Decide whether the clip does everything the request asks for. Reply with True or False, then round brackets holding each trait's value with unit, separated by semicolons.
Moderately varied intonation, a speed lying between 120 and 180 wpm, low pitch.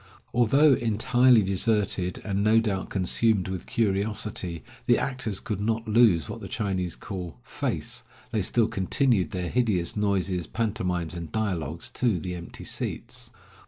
True (3.8 semitones; 140 wpm; 100 Hz)